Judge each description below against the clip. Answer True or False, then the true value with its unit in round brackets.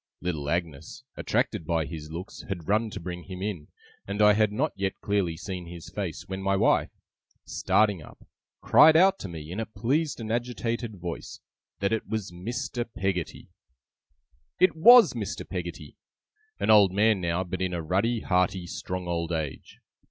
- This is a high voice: False (95 Hz)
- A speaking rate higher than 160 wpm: True (170 wpm)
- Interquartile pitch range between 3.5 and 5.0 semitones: True (4.2 semitones)